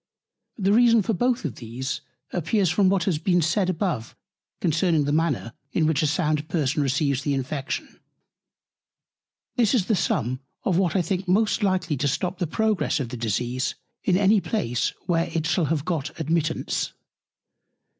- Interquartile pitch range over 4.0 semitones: Yes, average, 4.9 semitones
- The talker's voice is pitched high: No, medium, 165 Hz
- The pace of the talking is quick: No, average, 165 wpm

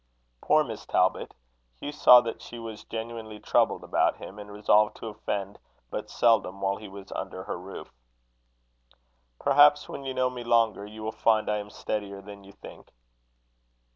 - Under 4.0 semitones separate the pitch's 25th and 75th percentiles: Yes, narrow, 2.5 semitones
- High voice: No, low, 110 Hz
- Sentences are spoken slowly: No, average, 170 wpm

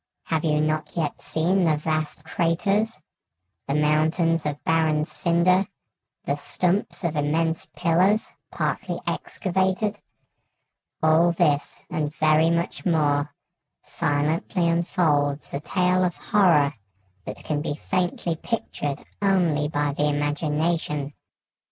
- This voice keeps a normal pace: No, slow, 115 wpm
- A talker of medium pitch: Yes, medium, 160 Hz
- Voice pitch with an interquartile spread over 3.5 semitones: No, average, 2.9 semitones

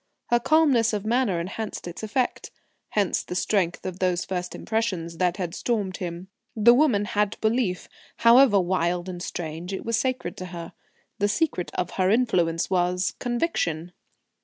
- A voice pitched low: No, high, 190 Hz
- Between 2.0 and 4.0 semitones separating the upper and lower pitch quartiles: No, average, 4.5 semitones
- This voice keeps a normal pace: Yes, average, 160 wpm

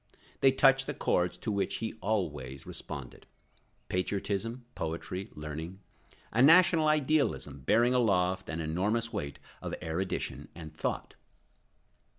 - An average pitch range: No, wide, 7.1 semitones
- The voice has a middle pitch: No, very low, 95 Hz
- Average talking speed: No, slow, 115 wpm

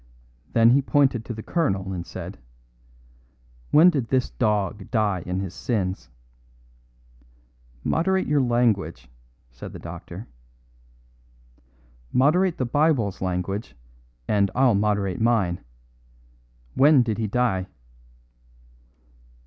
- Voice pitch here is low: Yes, low, 110 Hz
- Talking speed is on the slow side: Yes, slow, 105 wpm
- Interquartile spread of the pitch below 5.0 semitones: No, wide, 5.4 semitones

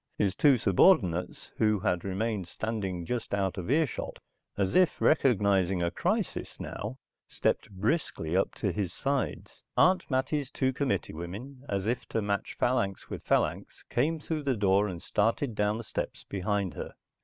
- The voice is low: Yes, low, 105 Hz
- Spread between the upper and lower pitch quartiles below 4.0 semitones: No, wide, 5.5 semitones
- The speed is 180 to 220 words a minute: No, average, 160 wpm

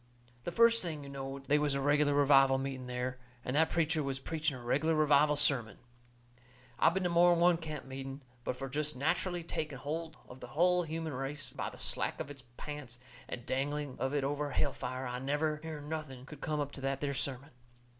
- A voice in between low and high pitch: Yes, medium, 145 Hz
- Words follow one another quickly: Yes, fast, 210 wpm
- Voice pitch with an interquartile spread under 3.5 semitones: Yes, narrow, 2.6 semitones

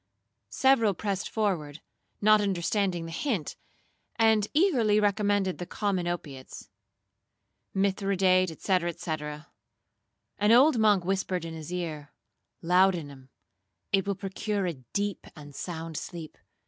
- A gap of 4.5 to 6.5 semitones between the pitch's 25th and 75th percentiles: No, average, 3.7 semitones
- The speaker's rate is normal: No, slow, 110 wpm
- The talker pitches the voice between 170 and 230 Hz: Yes, high, 190 Hz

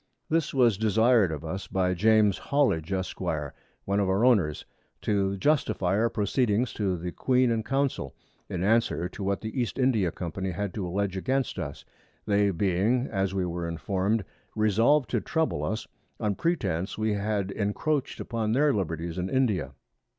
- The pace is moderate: Yes, average, 165 wpm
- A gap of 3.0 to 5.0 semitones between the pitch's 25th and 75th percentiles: Yes, average, 4.0 semitones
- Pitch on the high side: No, low, 100 Hz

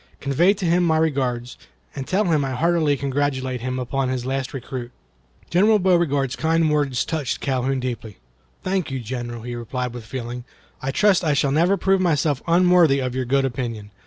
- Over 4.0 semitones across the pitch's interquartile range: Yes, average, 4.6 semitones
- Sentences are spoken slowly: No, average, 180 wpm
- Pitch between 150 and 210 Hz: No, low, 135 Hz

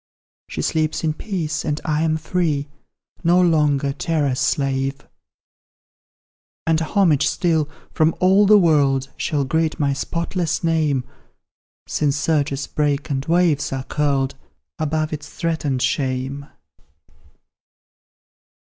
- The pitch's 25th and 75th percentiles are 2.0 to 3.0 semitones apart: Yes, average, 2.7 semitones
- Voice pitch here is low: No, medium, 150 Hz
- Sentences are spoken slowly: Yes, slow, 110 wpm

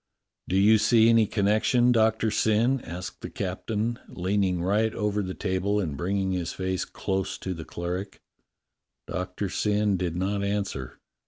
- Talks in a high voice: No, low, 100 Hz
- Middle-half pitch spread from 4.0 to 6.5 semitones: No, average, 2.7 semitones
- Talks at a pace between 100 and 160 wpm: Yes, average, 150 wpm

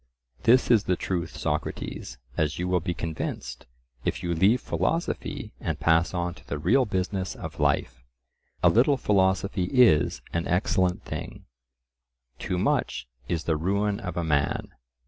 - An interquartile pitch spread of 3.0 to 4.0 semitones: Yes, average, 3.5 semitones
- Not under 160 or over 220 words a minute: No, average, 150 wpm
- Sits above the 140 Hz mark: No, very low, 90 Hz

